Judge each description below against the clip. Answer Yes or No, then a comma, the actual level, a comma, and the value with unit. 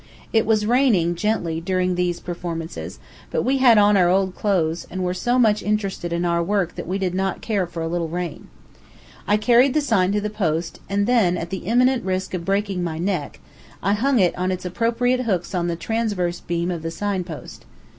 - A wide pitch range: No, average, 3.5 semitones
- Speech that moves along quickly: Yes, fast, 210 wpm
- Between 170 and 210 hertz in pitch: Yes, medium, 185 Hz